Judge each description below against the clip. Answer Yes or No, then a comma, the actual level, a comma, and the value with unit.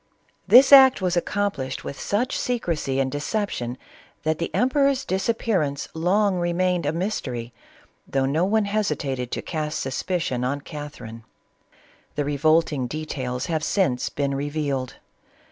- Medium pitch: Yes, medium, 155 Hz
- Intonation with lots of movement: Yes, wide, 6.2 semitones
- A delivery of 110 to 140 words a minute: Yes, slow, 135 wpm